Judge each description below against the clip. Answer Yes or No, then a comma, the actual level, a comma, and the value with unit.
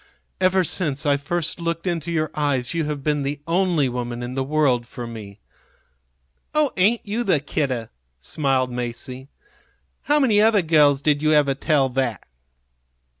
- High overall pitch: No, medium, 145 Hz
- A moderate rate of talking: Yes, average, 160 wpm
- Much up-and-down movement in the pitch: No, average, 4.5 semitones